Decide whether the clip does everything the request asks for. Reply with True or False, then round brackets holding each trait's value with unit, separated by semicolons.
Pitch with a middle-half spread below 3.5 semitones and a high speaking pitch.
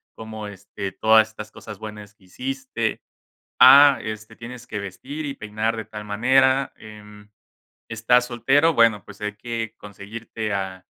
False (2.9 semitones; 110 Hz)